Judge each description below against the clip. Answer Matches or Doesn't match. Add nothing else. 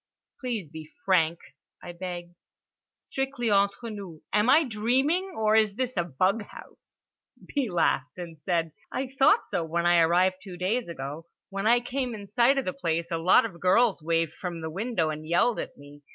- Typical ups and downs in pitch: Doesn't match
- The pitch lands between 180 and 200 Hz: Matches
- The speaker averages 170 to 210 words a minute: Matches